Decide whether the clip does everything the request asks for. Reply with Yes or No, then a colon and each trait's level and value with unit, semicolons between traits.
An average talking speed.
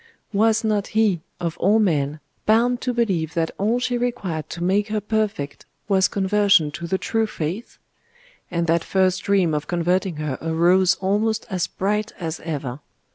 Yes: average, 165 wpm